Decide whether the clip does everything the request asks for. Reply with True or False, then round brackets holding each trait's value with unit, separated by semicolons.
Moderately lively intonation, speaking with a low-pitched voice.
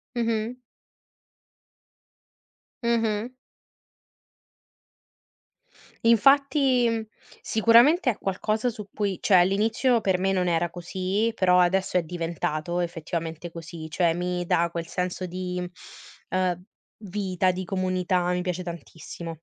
False (3.9 semitones; 185 Hz)